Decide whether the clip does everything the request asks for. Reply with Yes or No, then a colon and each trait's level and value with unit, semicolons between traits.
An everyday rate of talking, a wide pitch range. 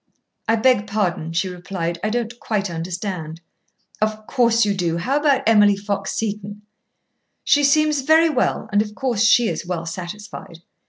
No: average, 160 wpm; average, 4.6 semitones